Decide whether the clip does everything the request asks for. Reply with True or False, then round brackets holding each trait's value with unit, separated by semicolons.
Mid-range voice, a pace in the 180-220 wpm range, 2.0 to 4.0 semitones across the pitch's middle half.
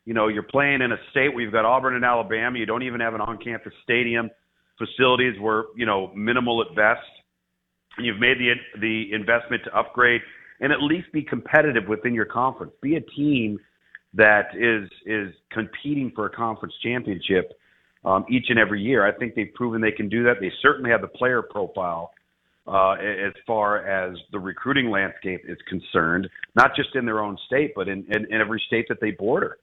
False (115 Hz; 200 wpm; 2.7 semitones)